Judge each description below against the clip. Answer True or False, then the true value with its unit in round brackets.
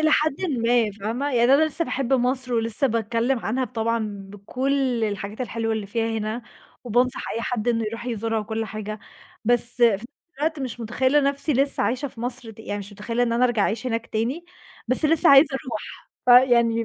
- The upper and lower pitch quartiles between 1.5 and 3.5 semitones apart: True (2.7 semitones)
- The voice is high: True (235 Hz)